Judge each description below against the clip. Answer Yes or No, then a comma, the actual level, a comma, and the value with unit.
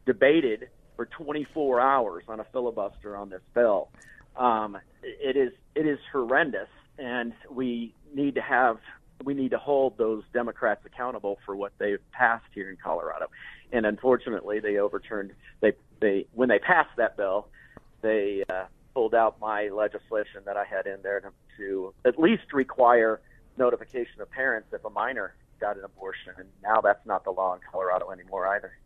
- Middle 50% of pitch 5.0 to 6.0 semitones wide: Yes, average, 5.3 semitones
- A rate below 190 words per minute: Yes, average, 170 wpm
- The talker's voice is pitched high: No, low, 120 Hz